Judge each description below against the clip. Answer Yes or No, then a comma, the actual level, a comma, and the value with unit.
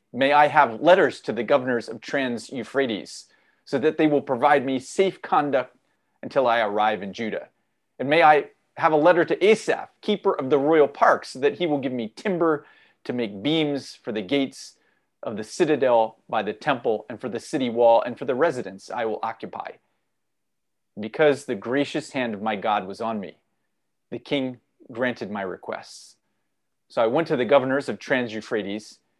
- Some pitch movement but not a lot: Yes, average, 4.1 semitones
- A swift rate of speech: No, average, 190 wpm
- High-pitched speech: No, low, 135 Hz